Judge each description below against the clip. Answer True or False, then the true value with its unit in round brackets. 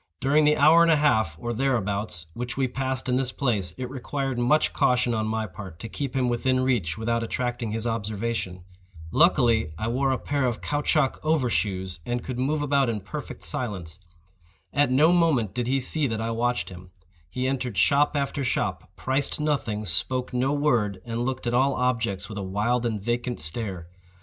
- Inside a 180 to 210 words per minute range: True (190 wpm)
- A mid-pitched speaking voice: False (120 Hz)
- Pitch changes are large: False (3.8 semitones)